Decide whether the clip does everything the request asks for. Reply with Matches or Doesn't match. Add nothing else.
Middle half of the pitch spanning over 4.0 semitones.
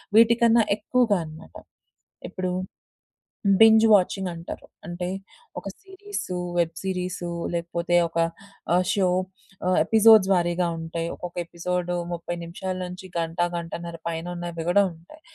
Doesn't match